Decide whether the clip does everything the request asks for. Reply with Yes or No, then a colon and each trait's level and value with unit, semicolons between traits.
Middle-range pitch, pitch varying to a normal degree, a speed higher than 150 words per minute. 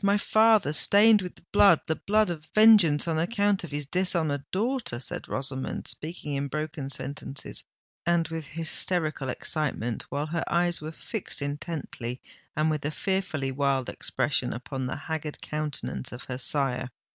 No: medium, 155 Hz; average, 4.3 semitones; average, 145 wpm